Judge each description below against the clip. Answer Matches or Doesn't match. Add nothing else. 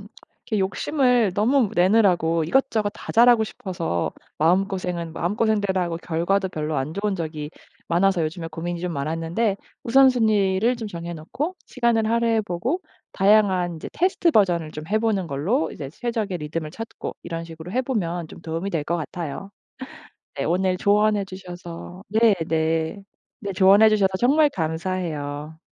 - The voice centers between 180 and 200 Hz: Matches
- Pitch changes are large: Doesn't match